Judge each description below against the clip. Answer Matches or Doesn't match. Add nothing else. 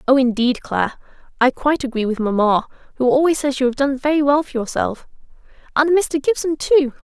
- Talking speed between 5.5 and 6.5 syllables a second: Matches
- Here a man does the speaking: Doesn't match